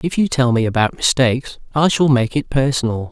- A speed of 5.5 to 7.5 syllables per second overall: Yes, 5.6 syllables/s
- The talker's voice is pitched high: No, low, 130 Hz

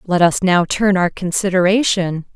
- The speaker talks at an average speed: Yes, average, 155 wpm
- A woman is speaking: Yes, female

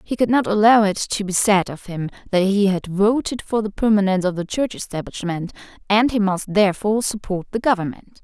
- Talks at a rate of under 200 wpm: No, fast, 205 wpm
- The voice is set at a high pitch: Yes, high, 205 Hz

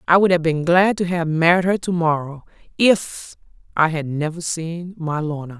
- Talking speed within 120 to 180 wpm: No, average, 195 wpm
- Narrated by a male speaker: No, female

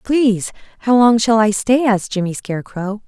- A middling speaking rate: Yes, average, 175 wpm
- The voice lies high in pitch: Yes, high, 220 Hz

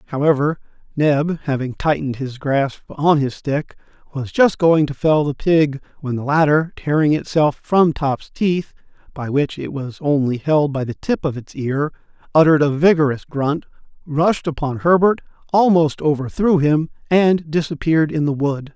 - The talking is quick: No, average, 165 wpm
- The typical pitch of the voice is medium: Yes, medium, 150 Hz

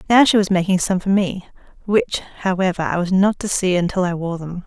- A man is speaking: No, female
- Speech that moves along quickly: Yes, fast, 230 wpm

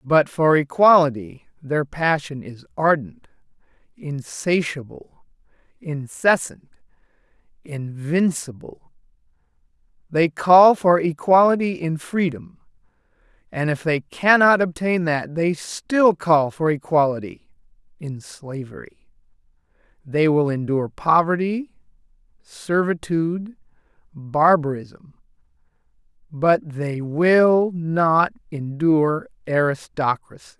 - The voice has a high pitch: No, medium, 160 Hz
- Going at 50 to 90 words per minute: Yes, slow, 80 wpm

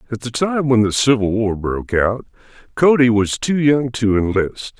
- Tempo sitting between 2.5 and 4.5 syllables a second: No, 4.7 syllables/s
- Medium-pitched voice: No, low, 120 Hz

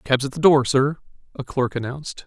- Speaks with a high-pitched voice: No, low, 135 Hz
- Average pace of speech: No, fast, 210 wpm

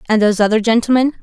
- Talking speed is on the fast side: No, average, 195 wpm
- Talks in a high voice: Yes, high, 225 Hz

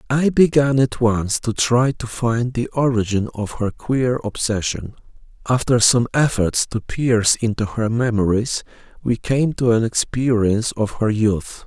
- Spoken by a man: Yes, male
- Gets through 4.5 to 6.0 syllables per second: No, 4.2 syllables/s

